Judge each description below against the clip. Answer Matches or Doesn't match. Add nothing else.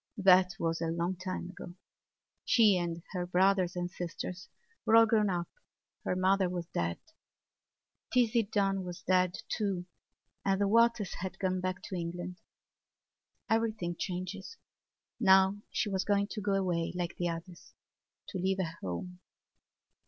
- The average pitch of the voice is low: Doesn't match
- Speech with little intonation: Matches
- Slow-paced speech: Doesn't match